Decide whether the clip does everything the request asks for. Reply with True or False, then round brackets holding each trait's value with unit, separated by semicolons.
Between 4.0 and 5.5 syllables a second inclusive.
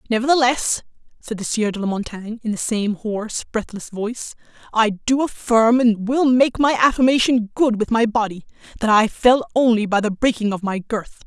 True (5.1 syllables/s)